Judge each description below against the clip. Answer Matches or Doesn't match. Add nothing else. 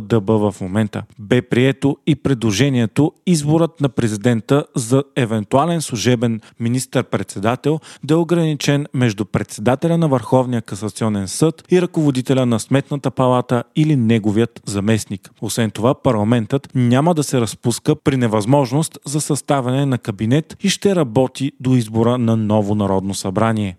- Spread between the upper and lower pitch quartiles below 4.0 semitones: Doesn't match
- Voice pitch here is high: Doesn't match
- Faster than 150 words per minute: Doesn't match